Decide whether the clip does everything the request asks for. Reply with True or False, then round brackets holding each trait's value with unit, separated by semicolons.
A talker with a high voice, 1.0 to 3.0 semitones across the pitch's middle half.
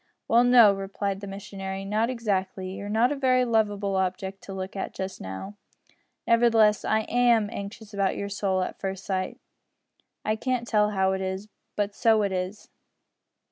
True (200 Hz; 2.5 semitones)